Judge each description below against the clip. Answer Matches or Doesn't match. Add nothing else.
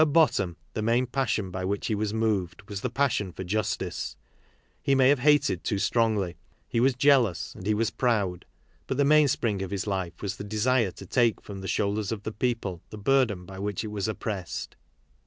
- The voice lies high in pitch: Doesn't match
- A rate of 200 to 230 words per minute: Matches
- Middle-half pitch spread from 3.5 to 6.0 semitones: Matches